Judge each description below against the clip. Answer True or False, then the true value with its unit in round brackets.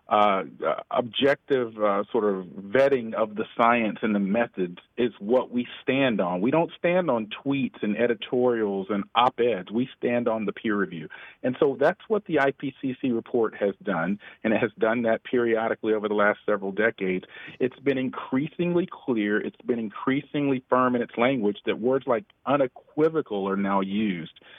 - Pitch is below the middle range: True (120 Hz)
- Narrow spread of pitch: False (4.3 semitones)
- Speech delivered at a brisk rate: False (175 wpm)